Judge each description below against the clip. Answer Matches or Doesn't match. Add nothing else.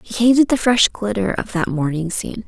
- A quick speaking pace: Matches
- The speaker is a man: Doesn't match